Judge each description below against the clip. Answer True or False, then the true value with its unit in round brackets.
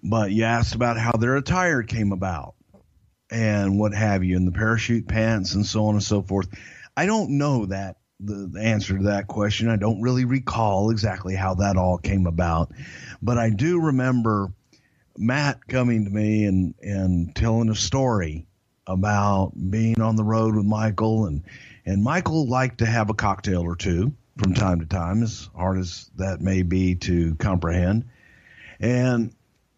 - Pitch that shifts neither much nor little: True (3.4 semitones)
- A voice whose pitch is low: True (105 Hz)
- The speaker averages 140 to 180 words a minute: True (175 wpm)